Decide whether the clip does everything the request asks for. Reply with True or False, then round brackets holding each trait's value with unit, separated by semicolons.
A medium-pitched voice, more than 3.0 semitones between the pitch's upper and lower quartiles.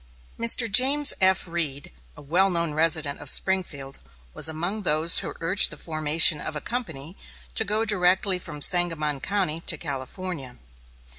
True (170 Hz; 4.1 semitones)